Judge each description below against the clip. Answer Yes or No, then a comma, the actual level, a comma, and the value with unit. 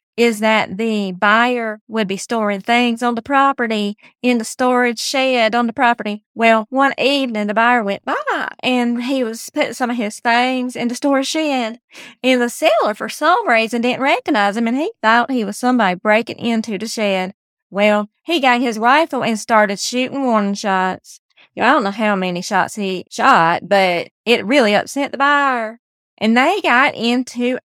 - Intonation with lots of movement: No, average, 3.0 semitones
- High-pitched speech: Yes, high, 235 Hz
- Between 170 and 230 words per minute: Yes, average, 185 wpm